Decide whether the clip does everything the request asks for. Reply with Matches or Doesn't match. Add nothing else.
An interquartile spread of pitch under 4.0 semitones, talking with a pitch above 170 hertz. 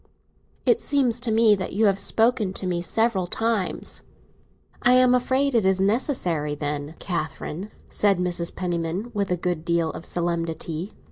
Doesn't match